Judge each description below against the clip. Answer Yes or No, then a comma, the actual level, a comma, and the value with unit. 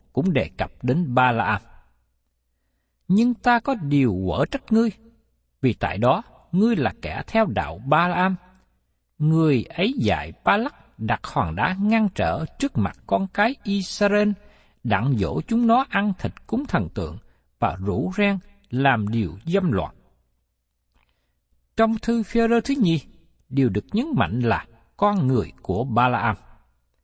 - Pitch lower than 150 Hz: Yes, medium, 140 Hz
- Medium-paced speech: No, slow, 160 wpm